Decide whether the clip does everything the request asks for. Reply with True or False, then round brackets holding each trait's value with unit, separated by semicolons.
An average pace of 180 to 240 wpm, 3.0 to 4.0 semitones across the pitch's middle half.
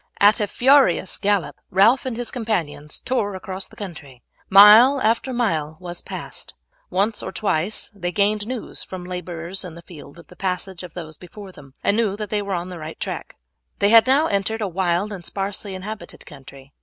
True (195 wpm; 3.7 semitones)